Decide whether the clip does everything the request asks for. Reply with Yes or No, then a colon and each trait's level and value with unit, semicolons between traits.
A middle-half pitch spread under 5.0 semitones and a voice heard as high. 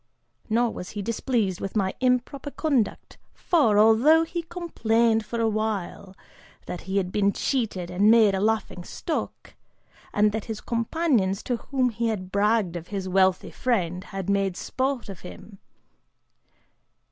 Yes: average, 3.9 semitones; high, 215 Hz